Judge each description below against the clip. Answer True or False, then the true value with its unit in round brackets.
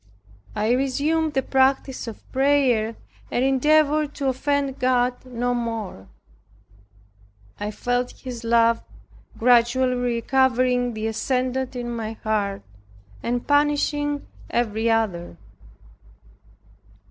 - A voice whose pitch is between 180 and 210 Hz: False (250 Hz)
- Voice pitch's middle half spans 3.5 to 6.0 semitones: False (2.6 semitones)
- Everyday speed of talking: False (100 wpm)